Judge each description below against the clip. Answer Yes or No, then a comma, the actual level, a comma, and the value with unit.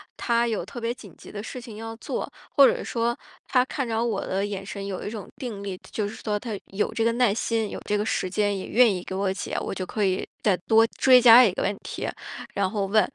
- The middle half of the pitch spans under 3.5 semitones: Yes, average, 2.8 semitones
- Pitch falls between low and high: No, high, 215 Hz